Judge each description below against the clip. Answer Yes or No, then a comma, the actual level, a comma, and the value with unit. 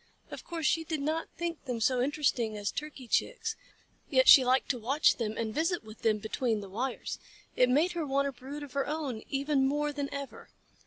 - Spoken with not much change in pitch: No, average, 3.7 semitones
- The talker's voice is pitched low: No, very high, 275 Hz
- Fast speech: Yes, fast, 210 wpm